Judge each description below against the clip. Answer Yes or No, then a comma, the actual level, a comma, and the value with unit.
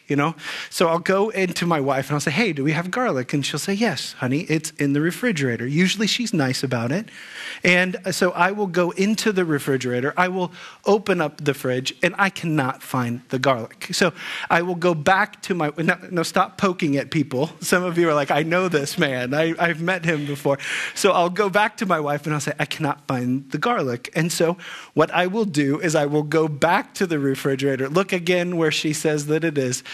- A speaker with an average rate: No, fast, 230 wpm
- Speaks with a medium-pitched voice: Yes, medium, 160 Hz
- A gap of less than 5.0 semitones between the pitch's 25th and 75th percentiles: Yes, average, 4.2 semitones